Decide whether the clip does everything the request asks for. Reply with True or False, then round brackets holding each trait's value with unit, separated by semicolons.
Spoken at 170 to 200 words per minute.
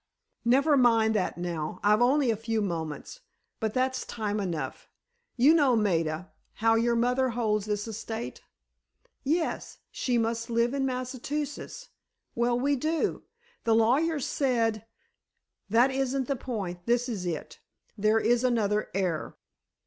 False (135 wpm)